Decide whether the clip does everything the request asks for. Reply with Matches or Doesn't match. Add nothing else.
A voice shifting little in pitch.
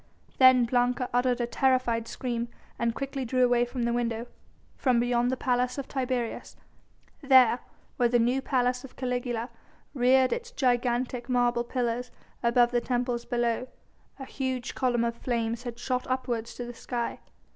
Matches